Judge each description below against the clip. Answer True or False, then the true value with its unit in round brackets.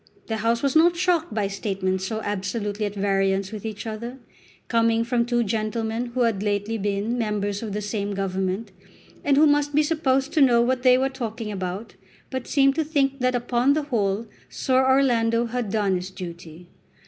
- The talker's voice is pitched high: True (225 Hz)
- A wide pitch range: False (4.2 semitones)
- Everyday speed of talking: True (185 wpm)